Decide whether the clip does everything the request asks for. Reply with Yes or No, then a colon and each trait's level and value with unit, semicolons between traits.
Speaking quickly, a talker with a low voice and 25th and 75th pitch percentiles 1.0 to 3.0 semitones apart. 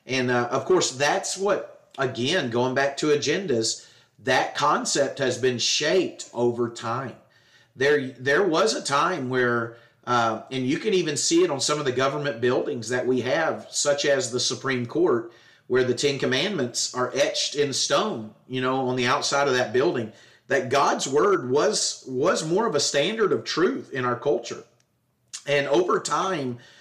No: average, 175 wpm; low, 130 Hz; average, 2.7 semitones